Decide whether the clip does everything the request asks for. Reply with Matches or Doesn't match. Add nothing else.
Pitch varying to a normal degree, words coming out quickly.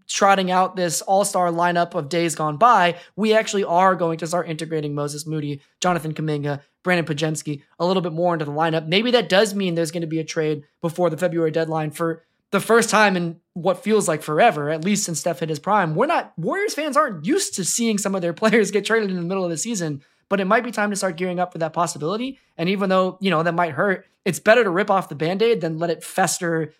Matches